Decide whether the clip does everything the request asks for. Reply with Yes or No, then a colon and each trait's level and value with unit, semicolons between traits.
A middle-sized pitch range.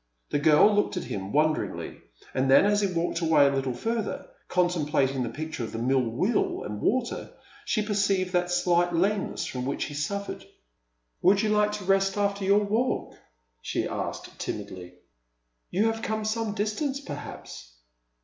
No: wide, 6.8 semitones